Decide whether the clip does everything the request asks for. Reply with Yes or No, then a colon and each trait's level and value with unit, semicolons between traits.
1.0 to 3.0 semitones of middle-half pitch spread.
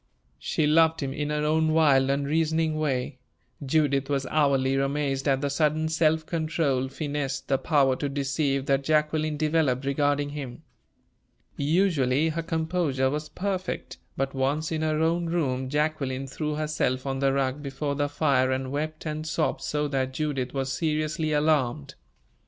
Yes: narrow, 2.5 semitones